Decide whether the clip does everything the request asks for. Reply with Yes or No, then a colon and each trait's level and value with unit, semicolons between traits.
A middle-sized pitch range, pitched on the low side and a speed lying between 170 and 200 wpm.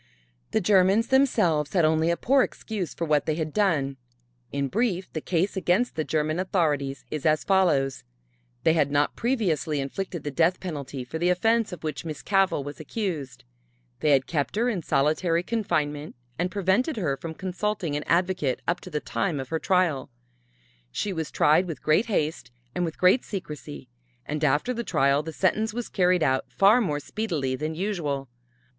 No: average, 4.6 semitones; medium, 165 Hz; average, 180 wpm